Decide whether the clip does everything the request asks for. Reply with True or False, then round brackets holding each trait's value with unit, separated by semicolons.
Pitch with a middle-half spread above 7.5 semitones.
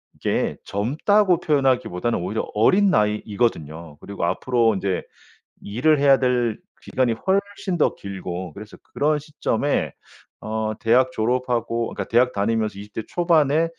False (5.6 semitones)